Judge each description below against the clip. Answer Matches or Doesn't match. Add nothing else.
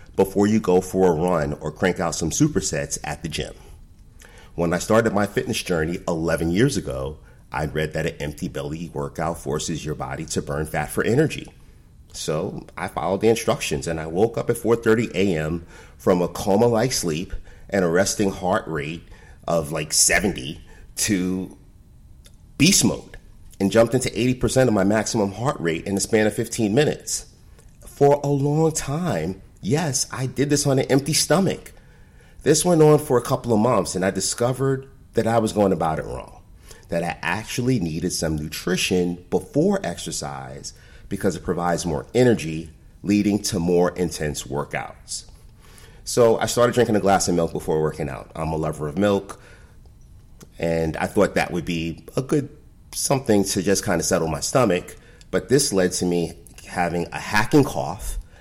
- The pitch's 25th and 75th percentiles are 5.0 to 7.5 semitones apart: Matches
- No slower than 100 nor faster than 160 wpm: Doesn't match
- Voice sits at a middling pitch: Doesn't match